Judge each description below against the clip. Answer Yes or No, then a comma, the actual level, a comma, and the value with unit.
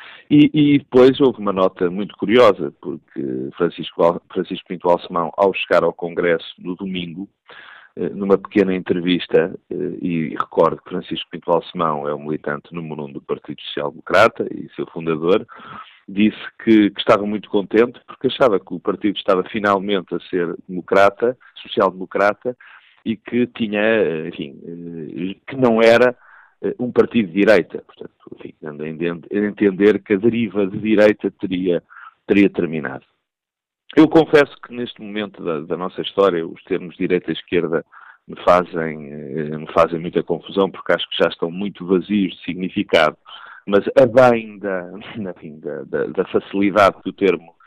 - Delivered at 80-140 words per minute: No, average, 150 wpm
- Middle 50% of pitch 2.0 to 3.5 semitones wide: No, average, 4.0 semitones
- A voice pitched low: Yes, low, 100 Hz